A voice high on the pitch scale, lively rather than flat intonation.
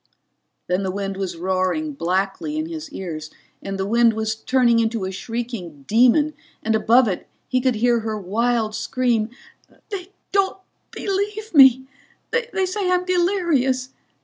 Yes: high, 240 Hz; wide, 7.7 semitones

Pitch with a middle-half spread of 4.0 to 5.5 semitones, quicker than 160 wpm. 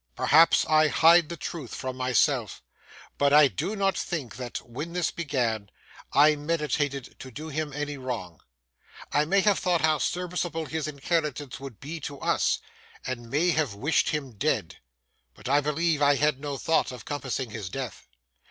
No: average, 3.6 semitones; average, 170 wpm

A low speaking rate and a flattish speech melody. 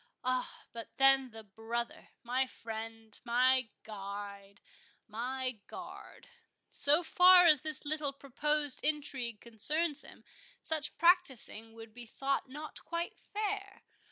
No: slow, 100 wpm; average, 5.2 semitones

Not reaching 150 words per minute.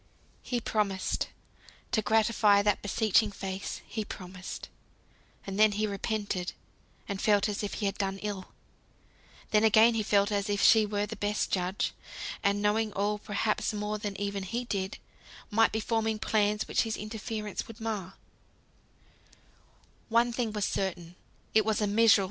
Yes: slow, 135 wpm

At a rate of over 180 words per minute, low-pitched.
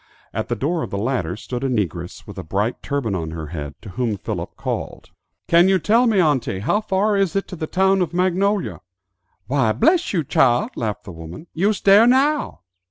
No: fast, 205 wpm; medium, 145 Hz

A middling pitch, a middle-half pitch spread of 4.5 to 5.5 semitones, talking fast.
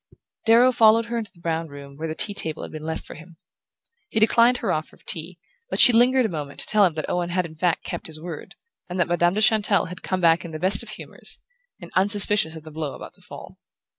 Yes: medium, 175 Hz; average, 5.0 semitones; fast, 255 wpm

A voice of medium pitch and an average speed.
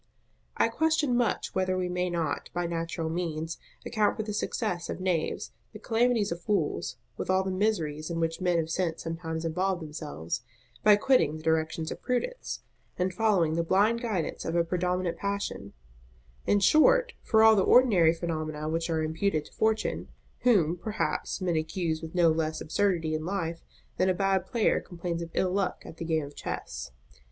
Yes: medium, 175 Hz; average, 180 wpm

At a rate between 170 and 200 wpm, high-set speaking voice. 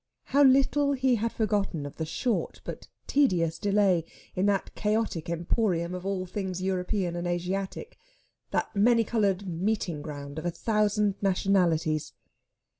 No: average, 140 wpm; high, 195 Hz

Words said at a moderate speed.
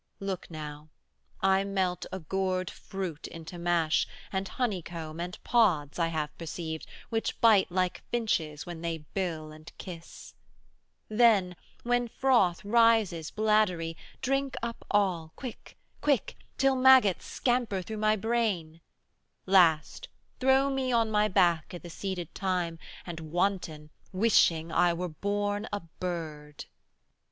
No: slow, 130 wpm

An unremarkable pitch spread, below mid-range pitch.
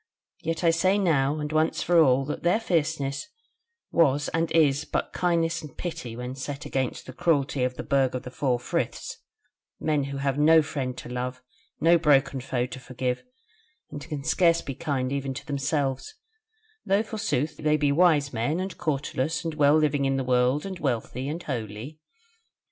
No: average, 3.5 semitones; medium, 145 Hz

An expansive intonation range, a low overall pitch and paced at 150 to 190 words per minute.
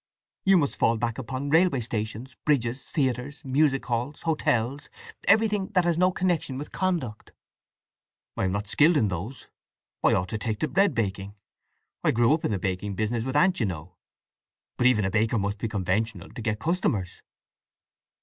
Yes: wide, 6.2 semitones; low, 120 Hz; average, 170 wpm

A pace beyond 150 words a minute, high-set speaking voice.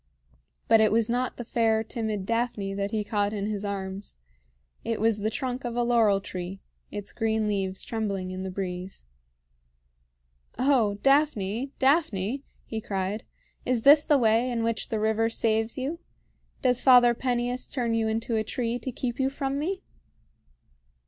Yes: average, 160 wpm; high, 225 Hz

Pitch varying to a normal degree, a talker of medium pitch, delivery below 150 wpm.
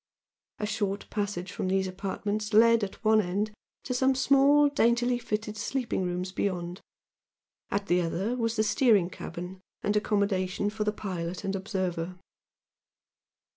No: average, 3.2 semitones; high, 205 Hz; average, 140 wpm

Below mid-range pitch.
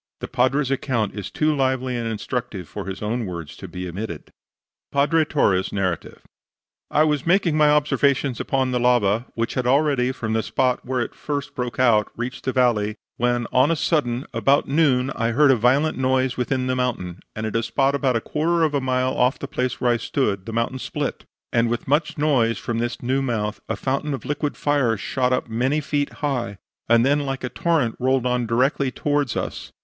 Yes: low, 125 Hz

